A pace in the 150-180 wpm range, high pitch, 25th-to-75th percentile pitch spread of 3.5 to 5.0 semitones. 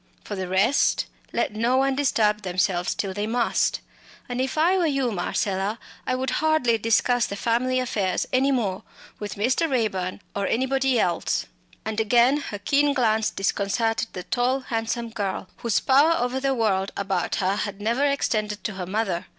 Yes: average, 170 wpm; high, 225 Hz; average, 4.4 semitones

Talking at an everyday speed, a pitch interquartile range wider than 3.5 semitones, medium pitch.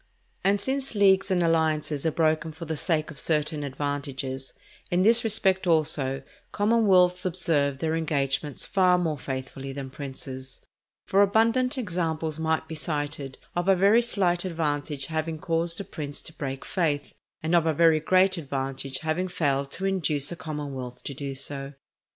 Yes: average, 160 wpm; average, 4.2 semitones; medium, 160 Hz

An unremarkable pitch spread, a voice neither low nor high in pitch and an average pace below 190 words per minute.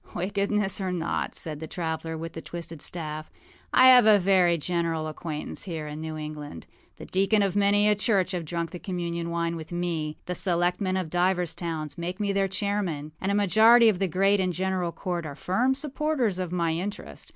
No: average, 3.3 semitones; medium, 180 Hz; average, 200 wpm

